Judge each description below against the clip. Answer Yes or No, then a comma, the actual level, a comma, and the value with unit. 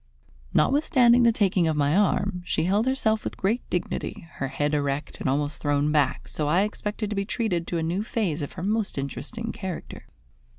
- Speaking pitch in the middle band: Yes, medium, 180 Hz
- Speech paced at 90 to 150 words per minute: No, average, 195 wpm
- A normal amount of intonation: No, wide, 6.6 semitones